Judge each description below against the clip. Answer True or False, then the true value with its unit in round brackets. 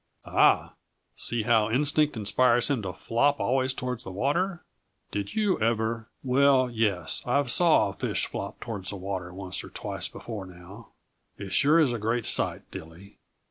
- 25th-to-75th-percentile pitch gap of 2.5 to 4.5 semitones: False (5.1 semitones)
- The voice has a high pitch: False (115 Hz)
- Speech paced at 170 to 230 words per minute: True (175 wpm)